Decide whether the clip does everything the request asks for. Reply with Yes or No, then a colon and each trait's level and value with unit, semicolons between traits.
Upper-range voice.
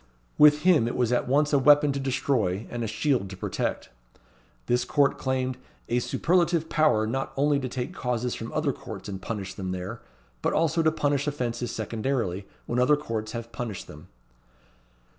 No: low, 125 Hz